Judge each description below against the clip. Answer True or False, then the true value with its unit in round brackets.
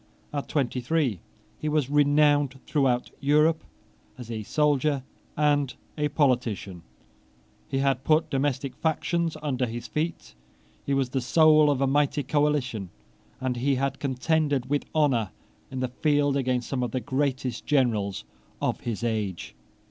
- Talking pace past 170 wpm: False (145 wpm)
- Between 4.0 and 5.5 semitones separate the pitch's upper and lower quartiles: False (2.9 semitones)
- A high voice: False (135 Hz)